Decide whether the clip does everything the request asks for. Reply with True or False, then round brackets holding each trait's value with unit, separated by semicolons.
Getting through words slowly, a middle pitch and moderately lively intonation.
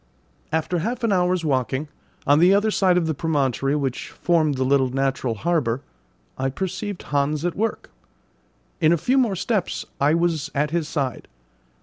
False (165 wpm; 160 Hz; 4.5 semitones)